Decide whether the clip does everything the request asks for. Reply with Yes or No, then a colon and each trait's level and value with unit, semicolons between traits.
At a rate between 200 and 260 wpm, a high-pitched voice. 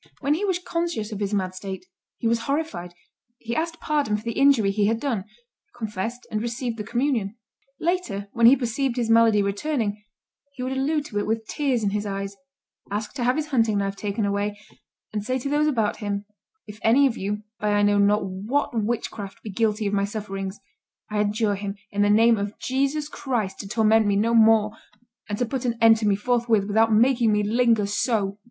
Yes: fast, 205 wpm; high, 220 Hz